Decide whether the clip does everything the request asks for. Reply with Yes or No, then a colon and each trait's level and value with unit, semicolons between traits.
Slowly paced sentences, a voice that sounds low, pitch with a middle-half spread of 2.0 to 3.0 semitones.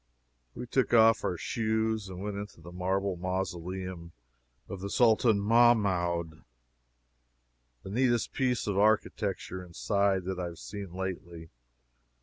No: slow, 130 wpm; very low, 95 Hz; average, 3.5 semitones